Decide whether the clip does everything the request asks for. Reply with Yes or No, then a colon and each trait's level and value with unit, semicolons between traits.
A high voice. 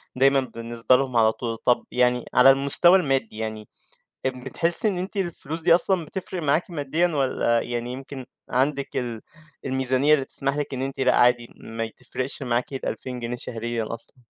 No: low, 130 Hz